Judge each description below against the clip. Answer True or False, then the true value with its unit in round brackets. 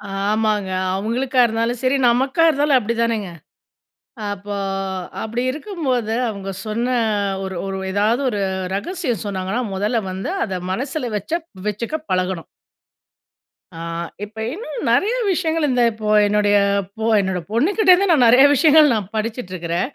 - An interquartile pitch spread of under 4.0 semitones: False (5.3 semitones)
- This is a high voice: True (230 Hz)